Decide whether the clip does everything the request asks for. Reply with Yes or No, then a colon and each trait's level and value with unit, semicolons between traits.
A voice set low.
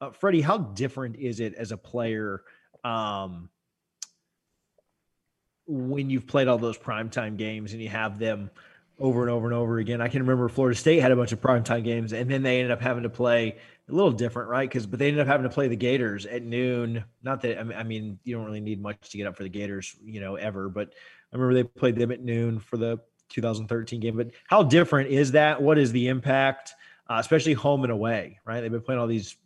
Yes: low, 120 Hz